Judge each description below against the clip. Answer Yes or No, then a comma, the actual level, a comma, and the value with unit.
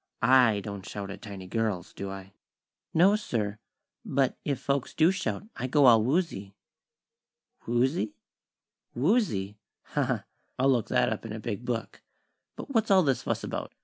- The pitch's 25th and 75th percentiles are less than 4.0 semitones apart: No, wide, 5.5 semitones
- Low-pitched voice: Yes, low, 120 Hz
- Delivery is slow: No, average, 160 wpm